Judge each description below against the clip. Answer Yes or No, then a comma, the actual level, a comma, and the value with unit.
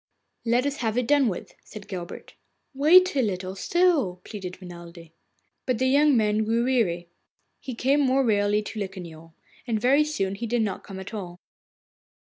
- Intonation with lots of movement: Yes, wide, 5.7 semitones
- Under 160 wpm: No, average, 170 wpm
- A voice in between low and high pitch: No, high, 220 Hz